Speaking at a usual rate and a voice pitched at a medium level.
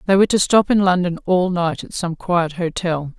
No: fast, 225 wpm; medium, 175 Hz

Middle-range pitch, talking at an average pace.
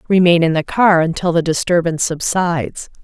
Yes: medium, 170 Hz; average, 160 wpm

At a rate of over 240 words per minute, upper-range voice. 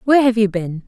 Yes: fast, 275 wpm; high, 215 Hz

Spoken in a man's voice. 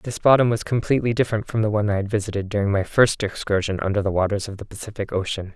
Yes: male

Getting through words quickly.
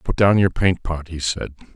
Yes: fast, 240 wpm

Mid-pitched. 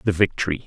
No: very low, 95 Hz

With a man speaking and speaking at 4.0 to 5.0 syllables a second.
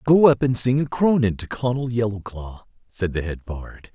Yes: male; 4.9 syllables/s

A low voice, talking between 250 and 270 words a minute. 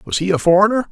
No: high, 200 Hz; fast, 260 wpm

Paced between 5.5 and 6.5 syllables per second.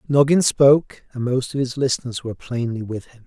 Yes: 5.7 syllables/s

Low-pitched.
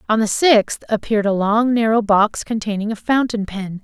No: high, 215 Hz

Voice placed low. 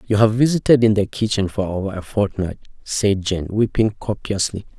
Yes: low, 105 Hz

